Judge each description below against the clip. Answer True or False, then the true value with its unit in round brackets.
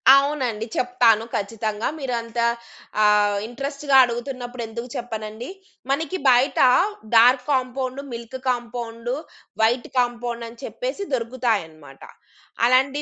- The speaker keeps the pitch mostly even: True (2.3 semitones)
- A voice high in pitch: True (240 Hz)